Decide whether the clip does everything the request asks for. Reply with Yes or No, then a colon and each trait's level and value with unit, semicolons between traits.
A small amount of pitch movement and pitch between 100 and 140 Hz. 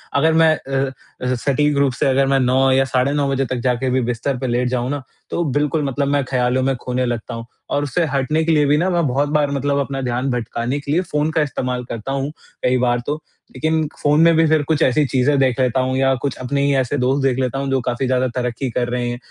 Yes: narrow, 2.3 semitones; low, 135 Hz